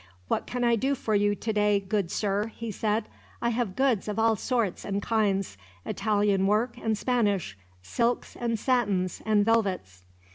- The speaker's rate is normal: Yes, average, 160 wpm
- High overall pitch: Yes, high, 210 Hz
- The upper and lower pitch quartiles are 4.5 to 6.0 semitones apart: No, narrow, 2.6 semitones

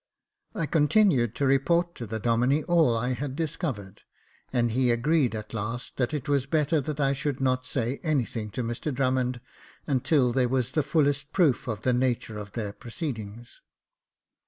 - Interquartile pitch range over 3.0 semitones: Yes, average, 3.8 semitones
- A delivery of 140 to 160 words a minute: No, average, 170 wpm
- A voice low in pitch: Yes, low, 130 Hz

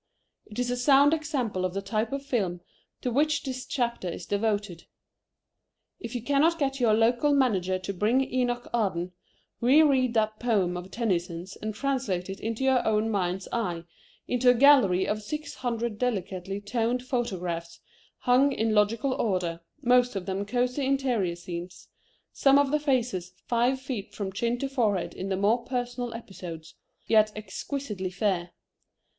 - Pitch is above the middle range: Yes, high, 225 Hz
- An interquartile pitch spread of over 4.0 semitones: Yes, average, 4.9 semitones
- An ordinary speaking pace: Yes, average, 160 wpm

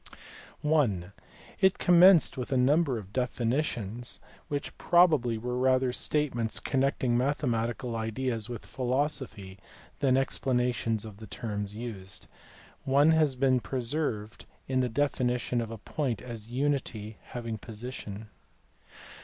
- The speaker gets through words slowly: Yes, slow, 120 wpm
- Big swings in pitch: No, average, 3.4 semitones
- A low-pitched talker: Yes, low, 125 Hz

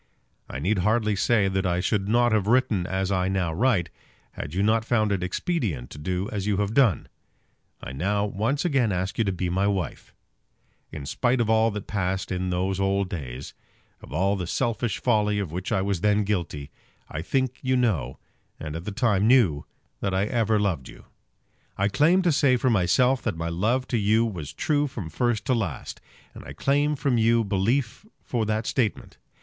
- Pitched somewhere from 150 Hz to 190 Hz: No, low, 100 Hz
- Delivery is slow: No, average, 200 wpm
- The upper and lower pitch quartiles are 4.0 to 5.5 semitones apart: Yes, average, 4.4 semitones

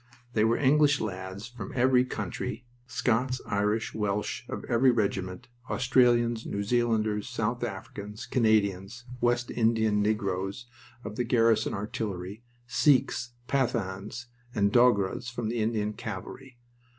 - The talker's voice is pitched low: Yes, low, 110 Hz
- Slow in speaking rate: Yes, slow, 120 wpm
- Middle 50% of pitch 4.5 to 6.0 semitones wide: No, average, 2.8 semitones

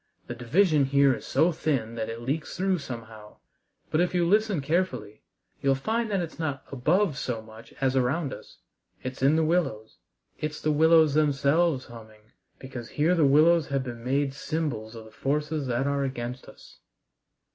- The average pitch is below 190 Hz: Yes, medium, 140 Hz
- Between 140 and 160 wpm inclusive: No, average, 170 wpm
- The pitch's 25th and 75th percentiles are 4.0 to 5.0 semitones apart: Yes, average, 4.7 semitones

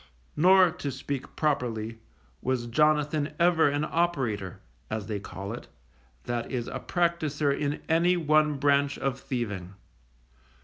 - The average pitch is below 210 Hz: Yes, medium, 140 Hz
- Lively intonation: No, average, 4.4 semitones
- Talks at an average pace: No, slow, 130 wpm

